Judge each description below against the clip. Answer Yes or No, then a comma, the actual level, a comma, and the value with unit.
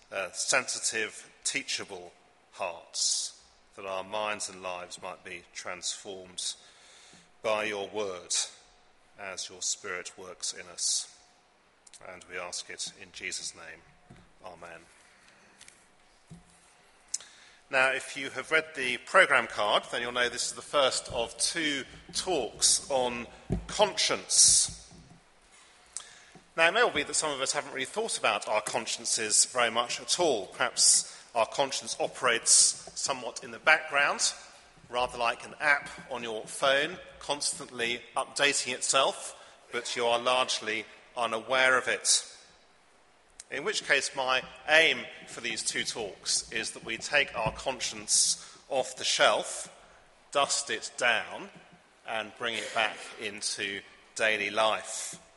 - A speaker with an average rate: No, slow, 130 wpm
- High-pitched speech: No, low, 130 Hz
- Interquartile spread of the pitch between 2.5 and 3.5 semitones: No, average, 4.1 semitones